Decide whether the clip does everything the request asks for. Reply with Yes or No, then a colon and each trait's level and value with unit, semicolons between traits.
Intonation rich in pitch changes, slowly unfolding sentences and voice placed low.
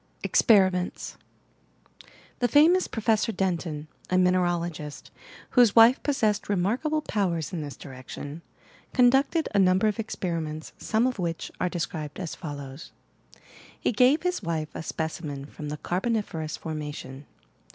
No: wide, 6.2 semitones; slow, 130 wpm; medium, 180 Hz